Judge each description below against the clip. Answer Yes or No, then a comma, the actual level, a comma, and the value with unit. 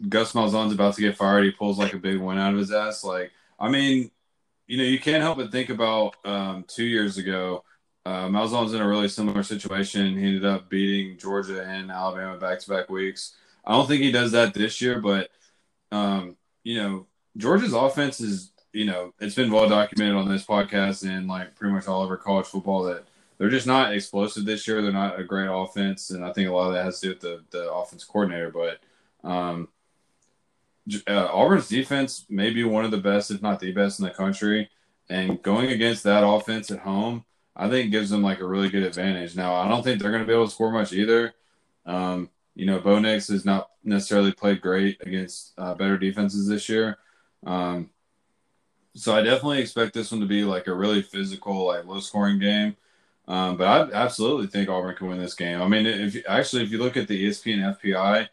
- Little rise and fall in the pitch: Yes, narrow, 2.2 semitones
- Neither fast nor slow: No, fast, 215 wpm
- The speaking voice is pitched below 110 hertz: Yes, low, 100 Hz